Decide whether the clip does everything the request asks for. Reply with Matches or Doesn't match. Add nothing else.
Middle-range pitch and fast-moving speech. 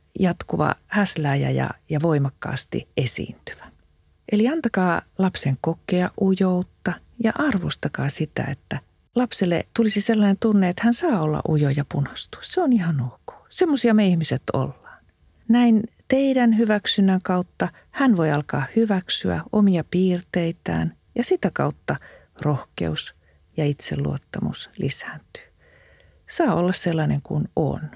Doesn't match